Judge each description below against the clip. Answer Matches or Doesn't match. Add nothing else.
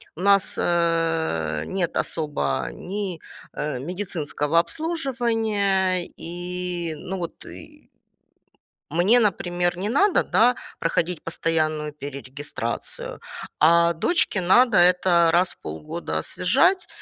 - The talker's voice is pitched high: Doesn't match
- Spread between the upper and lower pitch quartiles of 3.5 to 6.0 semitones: Matches